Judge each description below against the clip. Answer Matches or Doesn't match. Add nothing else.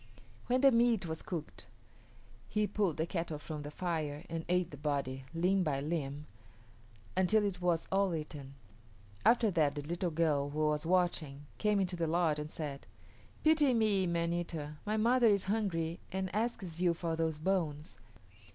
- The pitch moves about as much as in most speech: Matches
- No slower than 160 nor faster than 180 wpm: Matches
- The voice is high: Doesn't match